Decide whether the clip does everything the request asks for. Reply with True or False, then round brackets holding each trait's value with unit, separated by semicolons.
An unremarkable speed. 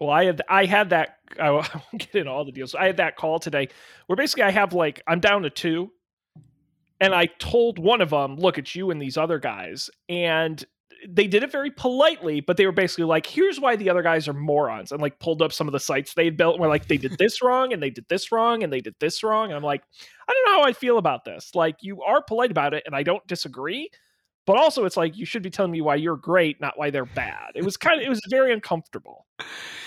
False (260 wpm)